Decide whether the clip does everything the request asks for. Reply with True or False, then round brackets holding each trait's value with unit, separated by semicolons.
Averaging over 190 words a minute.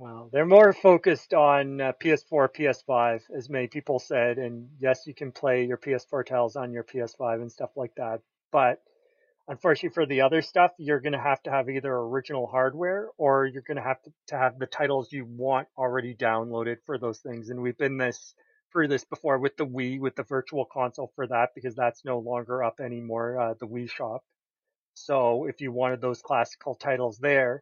True (200 wpm)